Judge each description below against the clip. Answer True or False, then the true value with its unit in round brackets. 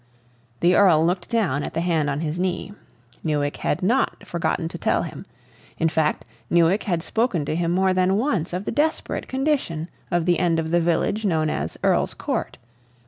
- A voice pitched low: False (175 Hz)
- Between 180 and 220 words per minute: True (190 wpm)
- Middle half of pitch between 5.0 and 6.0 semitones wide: False (3.0 semitones)